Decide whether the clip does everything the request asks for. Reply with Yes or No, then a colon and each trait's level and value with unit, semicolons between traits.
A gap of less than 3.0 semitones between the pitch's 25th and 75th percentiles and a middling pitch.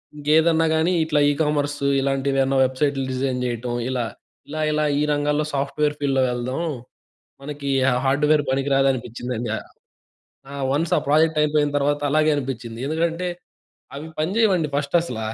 Yes: narrow, 2.4 semitones; medium, 145 Hz